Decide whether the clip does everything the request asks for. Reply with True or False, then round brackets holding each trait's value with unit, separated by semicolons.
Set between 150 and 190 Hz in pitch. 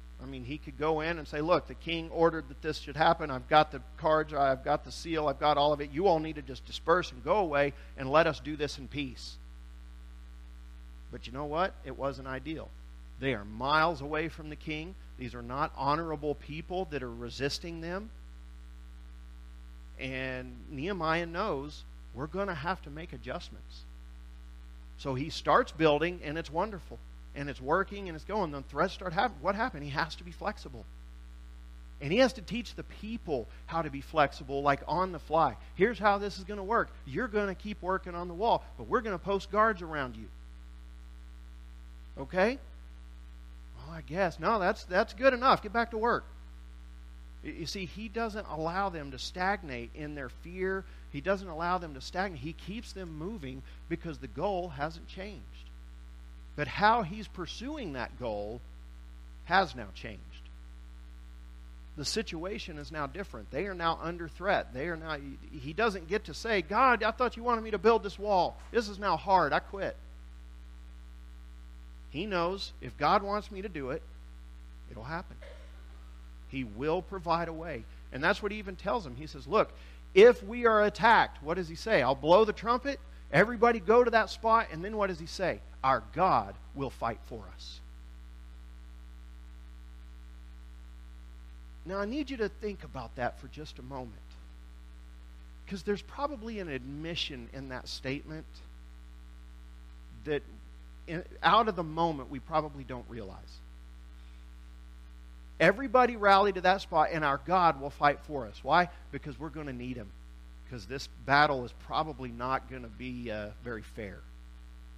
False (140 Hz)